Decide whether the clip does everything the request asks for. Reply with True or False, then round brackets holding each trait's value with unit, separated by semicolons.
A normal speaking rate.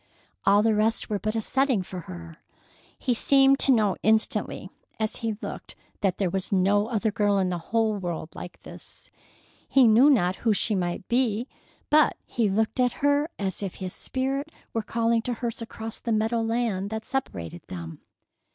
True (180 wpm)